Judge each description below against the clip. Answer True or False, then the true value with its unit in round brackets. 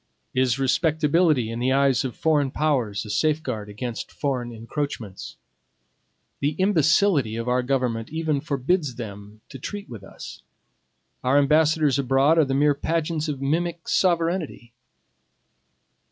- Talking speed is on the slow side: True (130 wpm)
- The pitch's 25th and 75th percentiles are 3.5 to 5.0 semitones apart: True (4.4 semitones)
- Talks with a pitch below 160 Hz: True (140 Hz)